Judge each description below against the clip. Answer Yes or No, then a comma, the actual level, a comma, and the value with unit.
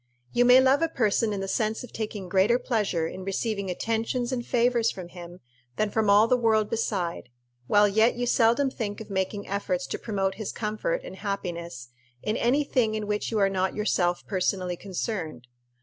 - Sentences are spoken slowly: No, average, 190 wpm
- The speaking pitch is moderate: No, high, 210 Hz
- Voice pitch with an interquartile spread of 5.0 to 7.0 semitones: No, average, 3.3 semitones